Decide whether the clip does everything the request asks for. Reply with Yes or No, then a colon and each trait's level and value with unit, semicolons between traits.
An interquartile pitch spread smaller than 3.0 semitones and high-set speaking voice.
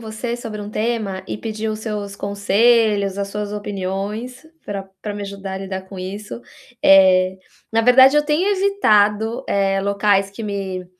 Yes: narrow, 2.4 semitones; high, 205 Hz